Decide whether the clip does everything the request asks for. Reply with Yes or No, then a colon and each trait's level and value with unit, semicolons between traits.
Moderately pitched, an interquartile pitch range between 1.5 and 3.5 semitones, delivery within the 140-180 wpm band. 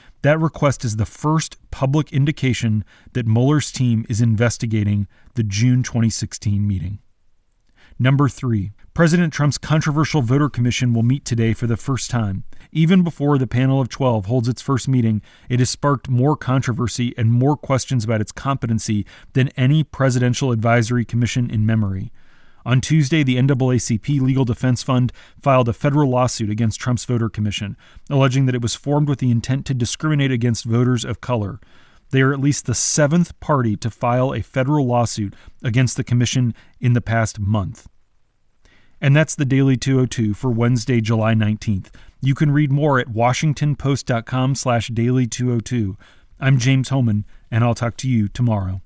No: low, 125 Hz; average, 3.2 semitones; average, 160 wpm